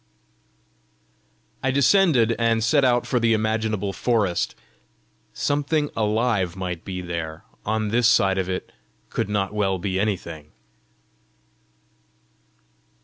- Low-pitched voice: Yes, low, 110 Hz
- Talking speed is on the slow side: Yes, slow, 110 wpm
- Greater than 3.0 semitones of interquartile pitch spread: Yes, average, 4.3 semitones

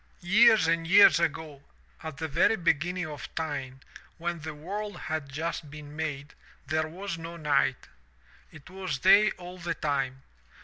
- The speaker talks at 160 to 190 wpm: No, average, 150 wpm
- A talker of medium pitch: Yes, medium, 160 Hz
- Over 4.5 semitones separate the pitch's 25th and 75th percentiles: No, average, 3.1 semitones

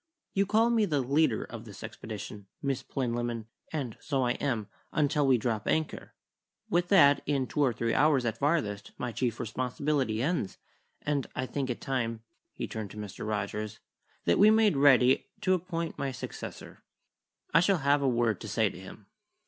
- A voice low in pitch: Yes, low, 130 Hz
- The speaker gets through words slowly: No, average, 180 wpm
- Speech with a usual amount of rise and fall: Yes, average, 4.7 semitones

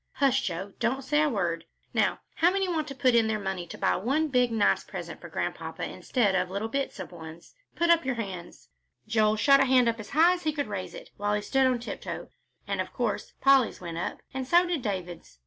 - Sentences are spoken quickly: Yes, fast, 230 wpm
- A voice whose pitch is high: Yes, high, 235 Hz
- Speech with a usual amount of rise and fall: No, wide, 6.0 semitones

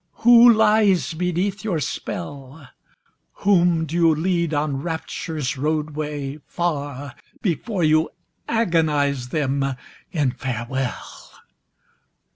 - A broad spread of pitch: No, average, 3.8 semitones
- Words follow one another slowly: Yes, slow, 90 wpm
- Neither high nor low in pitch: Yes, medium, 155 Hz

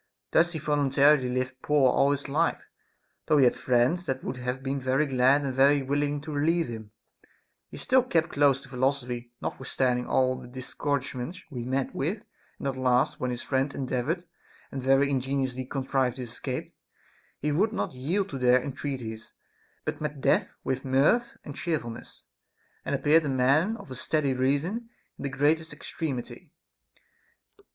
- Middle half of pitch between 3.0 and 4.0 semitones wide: No, narrow, 2.5 semitones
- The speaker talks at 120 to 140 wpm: No, average, 170 wpm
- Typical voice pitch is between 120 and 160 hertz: Yes, low, 135 Hz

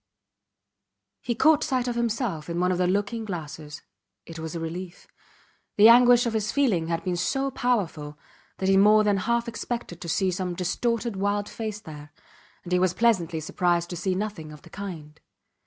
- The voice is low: No, high, 190 Hz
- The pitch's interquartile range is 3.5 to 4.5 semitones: No, average, 5.3 semitones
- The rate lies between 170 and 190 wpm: Yes, average, 185 wpm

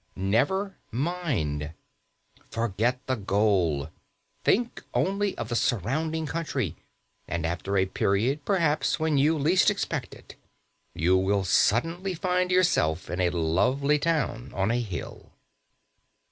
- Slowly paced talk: Yes, slow, 120 wpm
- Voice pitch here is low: Yes, low, 120 Hz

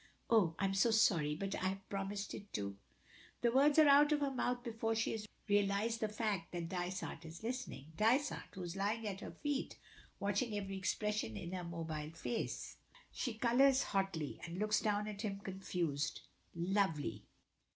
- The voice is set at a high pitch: Yes, high, 200 Hz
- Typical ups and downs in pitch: Yes, average, 4.2 semitones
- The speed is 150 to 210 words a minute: Yes, average, 180 wpm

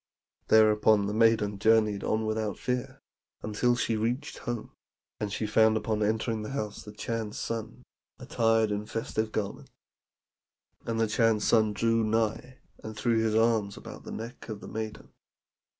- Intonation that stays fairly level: Yes, narrow, 1.1 semitones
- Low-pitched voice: Yes, low, 110 Hz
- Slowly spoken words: No, average, 155 wpm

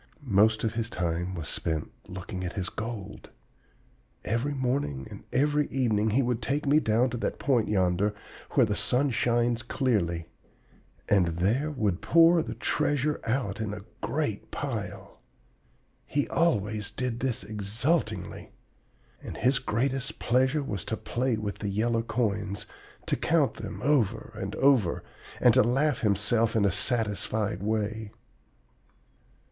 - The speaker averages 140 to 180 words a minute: Yes, average, 145 wpm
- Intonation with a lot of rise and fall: No, average, 4.2 semitones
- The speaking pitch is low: Yes, low, 115 Hz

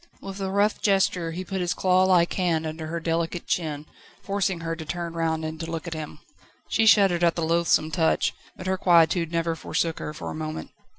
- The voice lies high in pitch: No, medium, 170 Hz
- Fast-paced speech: Yes, fast, 210 wpm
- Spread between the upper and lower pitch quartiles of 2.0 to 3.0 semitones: Yes, narrow, 2.4 semitones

